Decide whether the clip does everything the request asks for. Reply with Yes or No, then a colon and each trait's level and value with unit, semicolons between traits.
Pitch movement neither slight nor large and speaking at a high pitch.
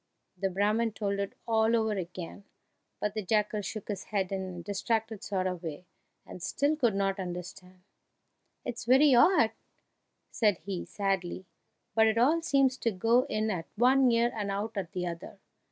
Yes: average, 3.6 semitones; high, 210 Hz